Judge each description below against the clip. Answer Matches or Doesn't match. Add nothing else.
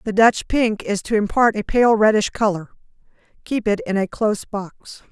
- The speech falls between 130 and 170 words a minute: Doesn't match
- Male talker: Doesn't match